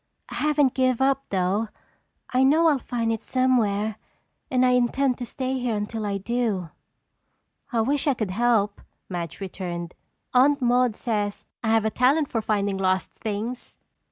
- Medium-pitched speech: No, high, 235 Hz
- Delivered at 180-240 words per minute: No, average, 160 wpm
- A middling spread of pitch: Yes, average, 4.0 semitones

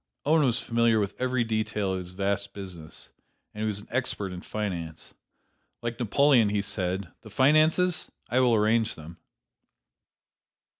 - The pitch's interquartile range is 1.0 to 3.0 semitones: No, average, 4.0 semitones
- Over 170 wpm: No, average, 150 wpm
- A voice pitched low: Yes, low, 105 Hz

